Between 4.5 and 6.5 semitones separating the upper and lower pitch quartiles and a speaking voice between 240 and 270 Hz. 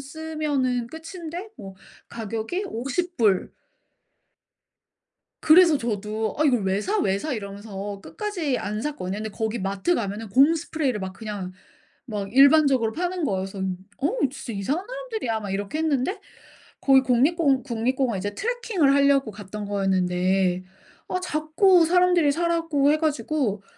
No: wide, 7.7 semitones; very high, 260 Hz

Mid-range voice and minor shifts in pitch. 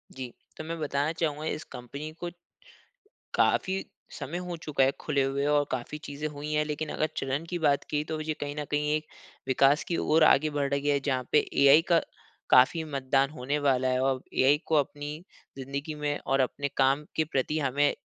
Yes: medium, 145 Hz; narrow, 2.1 semitones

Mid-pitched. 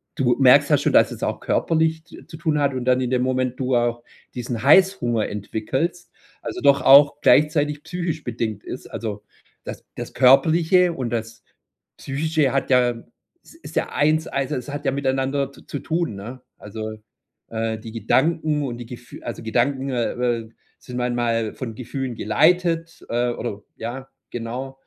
No: low, 130 Hz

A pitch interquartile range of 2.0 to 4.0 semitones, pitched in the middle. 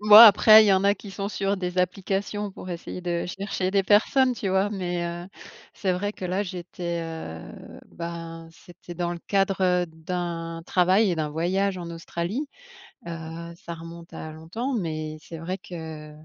Yes: average, 2.8 semitones; medium, 180 Hz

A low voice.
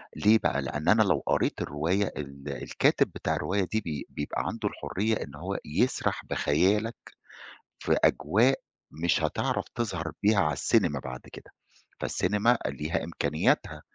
Yes: very low, 90 Hz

